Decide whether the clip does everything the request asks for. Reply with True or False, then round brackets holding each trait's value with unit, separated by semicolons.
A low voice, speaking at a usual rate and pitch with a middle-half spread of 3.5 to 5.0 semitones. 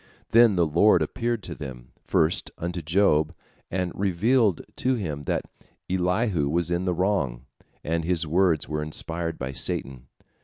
True (85 Hz; 150 wpm; 4.0 semitones)